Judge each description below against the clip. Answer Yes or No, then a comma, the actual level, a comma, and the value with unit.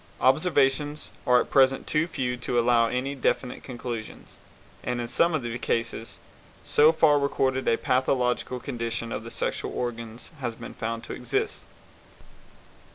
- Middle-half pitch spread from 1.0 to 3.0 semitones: Yes, average, 2.7 semitones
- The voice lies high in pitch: No, low, 125 Hz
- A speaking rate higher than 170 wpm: No, average, 150 wpm